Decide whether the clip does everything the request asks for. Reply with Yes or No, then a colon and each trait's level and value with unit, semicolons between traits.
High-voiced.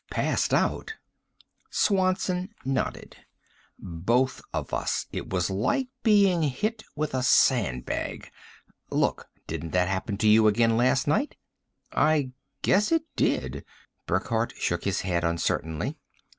No: low, 125 Hz